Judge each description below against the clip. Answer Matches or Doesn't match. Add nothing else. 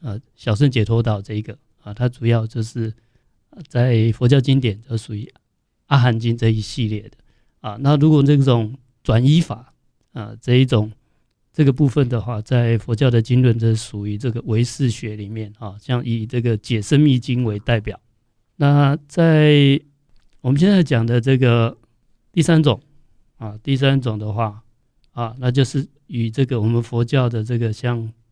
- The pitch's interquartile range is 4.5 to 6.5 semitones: Doesn't match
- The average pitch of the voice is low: Matches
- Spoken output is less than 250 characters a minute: Matches